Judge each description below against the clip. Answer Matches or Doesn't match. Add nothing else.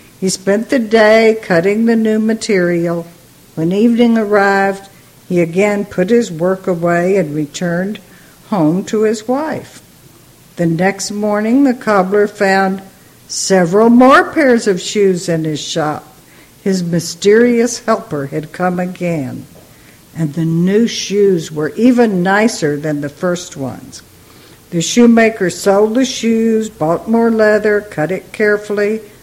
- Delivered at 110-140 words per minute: Matches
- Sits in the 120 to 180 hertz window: Doesn't match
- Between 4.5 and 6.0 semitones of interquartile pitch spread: Doesn't match